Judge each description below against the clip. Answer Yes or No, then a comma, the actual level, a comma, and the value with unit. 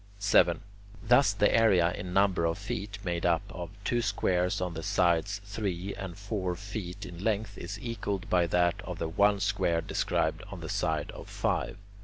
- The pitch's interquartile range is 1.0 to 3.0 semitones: Yes, average, 2.7 semitones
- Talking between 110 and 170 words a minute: No, average, 185 wpm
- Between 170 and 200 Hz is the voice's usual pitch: No, very low, 95 Hz